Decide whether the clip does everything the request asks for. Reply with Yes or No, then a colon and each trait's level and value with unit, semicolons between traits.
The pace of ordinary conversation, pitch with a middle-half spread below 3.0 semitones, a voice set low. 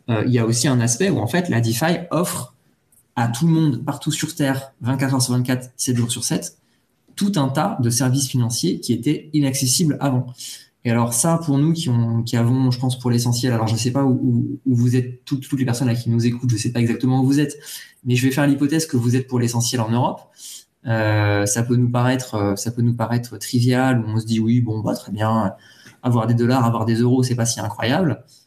No: fast, 250 wpm; narrow, 2.5 semitones; low, 125 Hz